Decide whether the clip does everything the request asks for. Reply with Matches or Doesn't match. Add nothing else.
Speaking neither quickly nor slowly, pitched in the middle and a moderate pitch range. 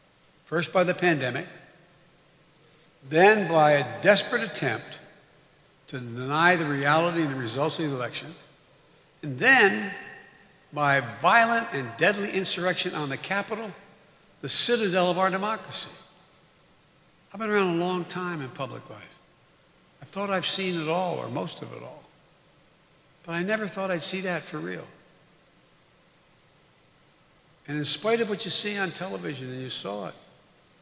Matches